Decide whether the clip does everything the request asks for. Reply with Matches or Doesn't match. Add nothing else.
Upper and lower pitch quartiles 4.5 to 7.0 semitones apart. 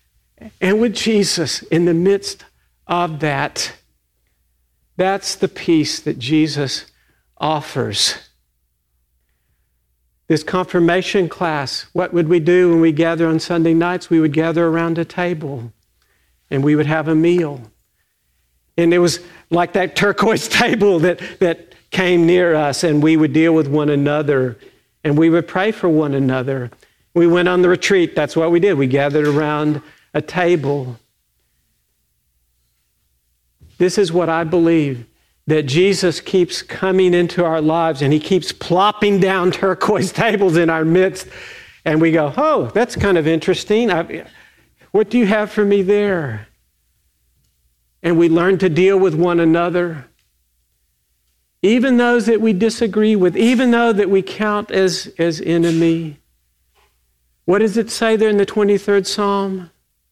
Matches